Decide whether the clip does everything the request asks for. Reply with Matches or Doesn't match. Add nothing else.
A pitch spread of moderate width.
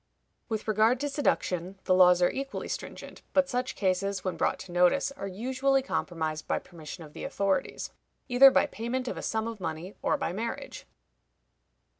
Doesn't match